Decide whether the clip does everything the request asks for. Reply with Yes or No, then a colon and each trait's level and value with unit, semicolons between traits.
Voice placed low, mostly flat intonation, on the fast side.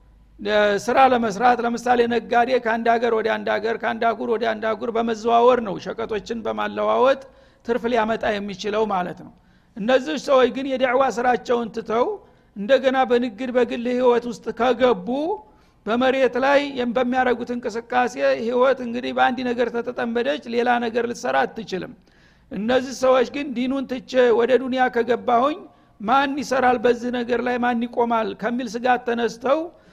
No: high, 245 Hz; narrow, 1.8 semitones; fast, 130 wpm